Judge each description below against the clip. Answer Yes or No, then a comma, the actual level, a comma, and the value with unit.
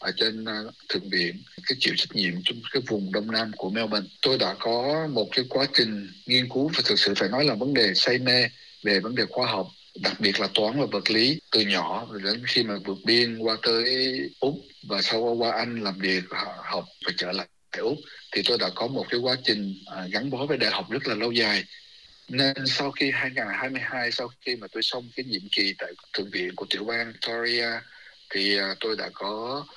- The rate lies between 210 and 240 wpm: Yes, average, 220 wpm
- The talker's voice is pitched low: Yes, low, 115 Hz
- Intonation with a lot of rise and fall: No, average, 3.1 semitones